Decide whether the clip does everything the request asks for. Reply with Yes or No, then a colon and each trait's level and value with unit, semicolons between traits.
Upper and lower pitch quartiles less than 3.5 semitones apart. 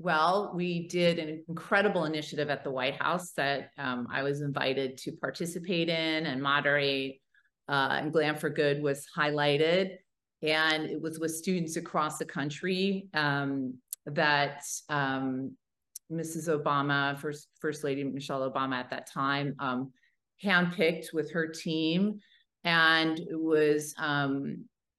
Yes: average, 2.7 semitones